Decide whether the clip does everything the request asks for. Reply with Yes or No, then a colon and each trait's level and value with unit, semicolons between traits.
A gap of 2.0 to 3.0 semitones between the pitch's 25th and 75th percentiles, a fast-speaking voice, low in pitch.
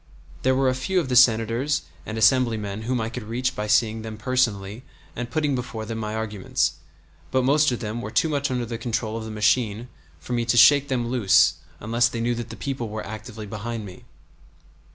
Yes: narrow, 2.6 semitones; fast, 210 wpm; low, 115 Hz